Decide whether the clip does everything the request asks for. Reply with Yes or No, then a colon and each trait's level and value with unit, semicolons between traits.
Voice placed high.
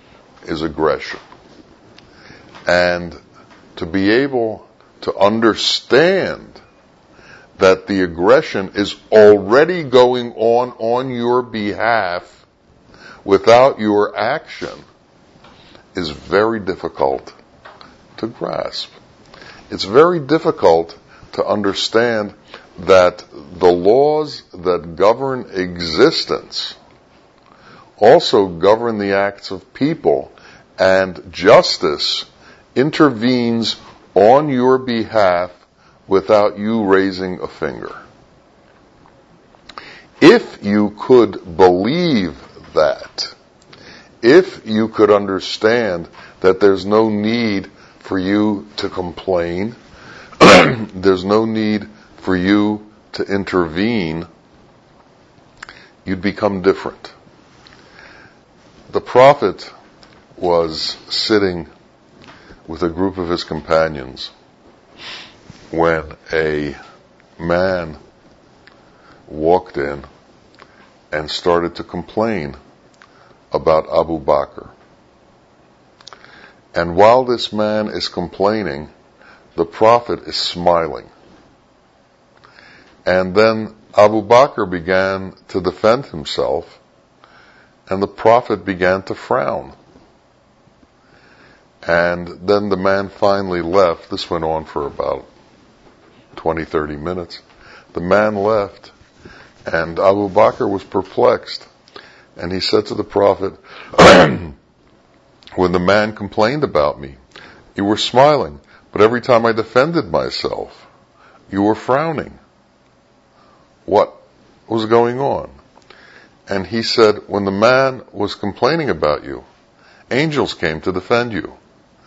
No: low, 100 Hz